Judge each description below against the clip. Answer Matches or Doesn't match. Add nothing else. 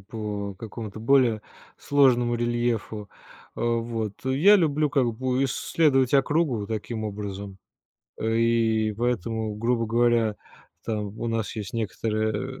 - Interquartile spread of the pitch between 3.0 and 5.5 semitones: Doesn't match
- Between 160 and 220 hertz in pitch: Doesn't match